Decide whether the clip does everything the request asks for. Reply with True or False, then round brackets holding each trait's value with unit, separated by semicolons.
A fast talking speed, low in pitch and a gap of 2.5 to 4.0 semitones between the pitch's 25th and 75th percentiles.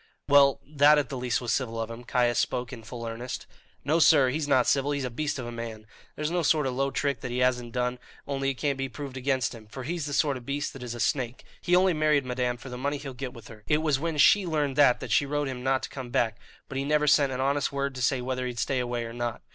True (280 wpm; 130 Hz; 2.8 semitones)